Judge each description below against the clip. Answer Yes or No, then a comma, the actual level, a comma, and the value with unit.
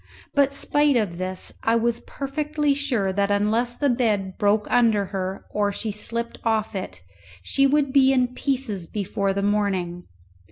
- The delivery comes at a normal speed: Yes, average, 160 wpm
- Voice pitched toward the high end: Yes, high, 220 Hz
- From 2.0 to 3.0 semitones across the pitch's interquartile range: No, average, 5.1 semitones